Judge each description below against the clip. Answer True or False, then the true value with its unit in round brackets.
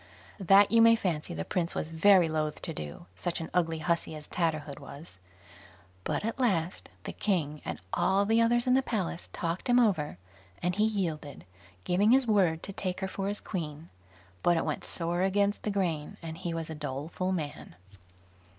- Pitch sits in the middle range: True (175 Hz)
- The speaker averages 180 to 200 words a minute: True (185 wpm)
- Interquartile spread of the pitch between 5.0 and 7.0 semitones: False (4.2 semitones)